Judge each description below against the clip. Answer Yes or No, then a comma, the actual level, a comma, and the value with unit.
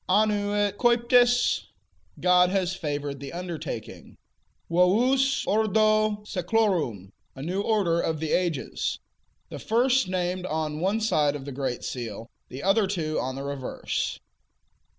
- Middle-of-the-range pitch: Yes, medium, 180 Hz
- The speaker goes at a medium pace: No, slow, 125 wpm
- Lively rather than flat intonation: Yes, wide, 6.3 semitones